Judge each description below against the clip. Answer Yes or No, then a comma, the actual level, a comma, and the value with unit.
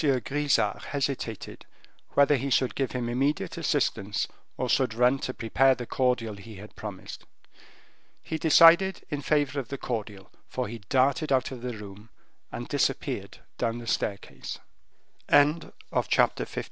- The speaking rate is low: No, average, 145 wpm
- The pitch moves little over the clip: No, average, 3.8 semitones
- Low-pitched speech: Yes, low, 130 Hz